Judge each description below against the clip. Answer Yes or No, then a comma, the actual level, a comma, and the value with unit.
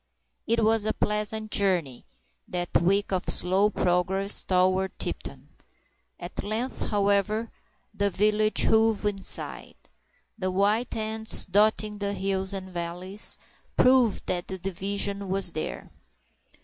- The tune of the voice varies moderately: No, narrow, 2.3 semitones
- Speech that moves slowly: Yes, slow, 120 wpm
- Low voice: No, high, 200 Hz